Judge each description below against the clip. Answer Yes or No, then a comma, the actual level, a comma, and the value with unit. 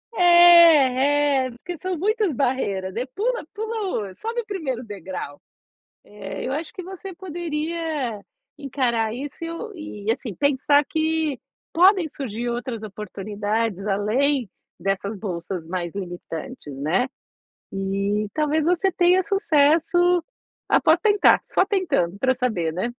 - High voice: Yes, very high, 270 Hz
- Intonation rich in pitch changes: Yes, wide, 8.5 semitones